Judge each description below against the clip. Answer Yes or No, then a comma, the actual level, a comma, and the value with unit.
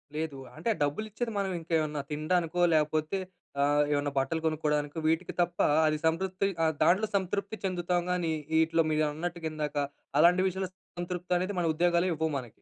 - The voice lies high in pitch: No, medium, 165 Hz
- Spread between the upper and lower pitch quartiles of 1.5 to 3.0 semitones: Yes, average, 2.7 semitones